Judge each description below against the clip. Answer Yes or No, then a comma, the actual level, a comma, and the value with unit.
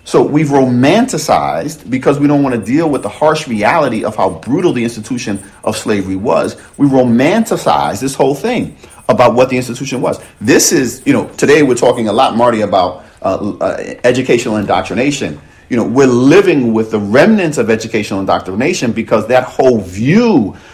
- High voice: No, low, 125 Hz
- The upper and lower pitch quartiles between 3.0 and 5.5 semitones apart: Yes, average, 4.3 semitones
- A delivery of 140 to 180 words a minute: Yes, average, 175 wpm